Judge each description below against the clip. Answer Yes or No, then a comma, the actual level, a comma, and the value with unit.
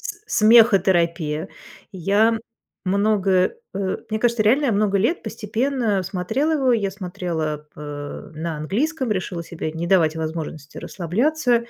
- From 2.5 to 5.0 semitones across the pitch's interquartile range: No, wide, 5.5 semitones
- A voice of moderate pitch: No, high, 195 Hz